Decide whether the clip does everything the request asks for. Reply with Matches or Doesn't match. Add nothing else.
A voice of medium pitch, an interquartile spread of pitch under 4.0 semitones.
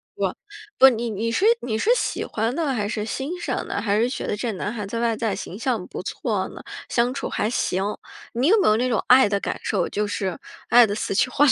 Doesn't match